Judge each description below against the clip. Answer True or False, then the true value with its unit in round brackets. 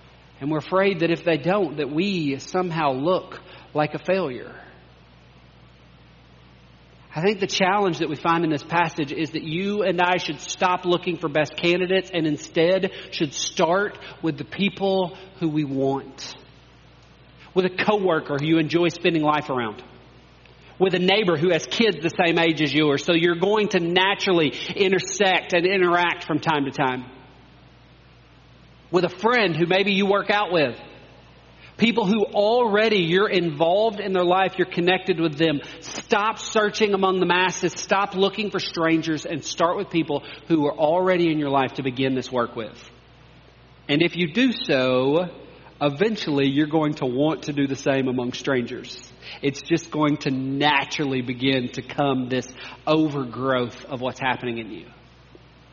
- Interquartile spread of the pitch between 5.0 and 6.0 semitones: True (5.4 semitones)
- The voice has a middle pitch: True (160 Hz)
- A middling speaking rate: True (165 wpm)